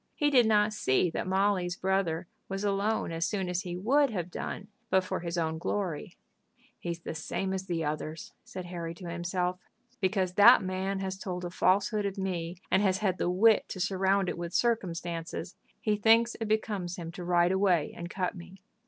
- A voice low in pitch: No, medium, 185 Hz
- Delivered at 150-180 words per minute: No, average, 195 wpm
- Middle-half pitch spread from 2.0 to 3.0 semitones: Yes, narrow, 2.4 semitones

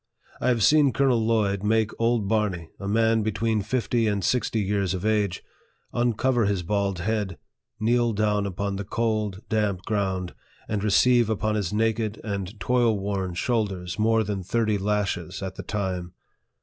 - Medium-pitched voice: No, low, 105 Hz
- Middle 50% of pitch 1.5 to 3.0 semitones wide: Yes, narrow, 2.4 semitones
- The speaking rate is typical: Yes, average, 160 wpm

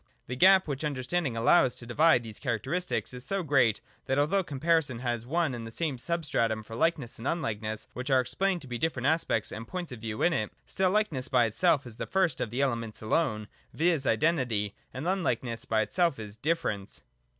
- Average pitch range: No, wide, 6.4 semitones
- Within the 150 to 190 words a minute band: No, average, 200 wpm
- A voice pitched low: Yes, low, 130 Hz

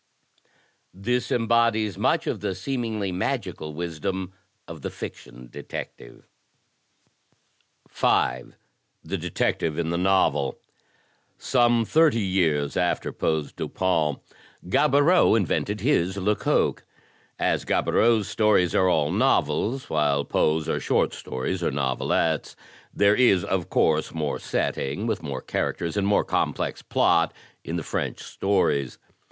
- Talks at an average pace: No, slow, 120 wpm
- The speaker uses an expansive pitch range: Yes, wide, 5.8 semitones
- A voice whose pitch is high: No, very low, 95 Hz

